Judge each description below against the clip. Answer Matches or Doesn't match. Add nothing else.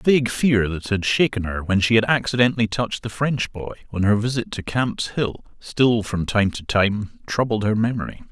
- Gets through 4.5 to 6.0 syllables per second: Matches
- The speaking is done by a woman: Doesn't match